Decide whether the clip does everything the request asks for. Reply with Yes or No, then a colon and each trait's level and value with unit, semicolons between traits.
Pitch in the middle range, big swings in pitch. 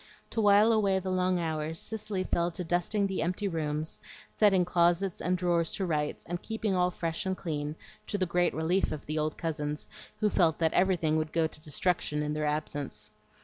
No: medium, 175 Hz; average, 3.3 semitones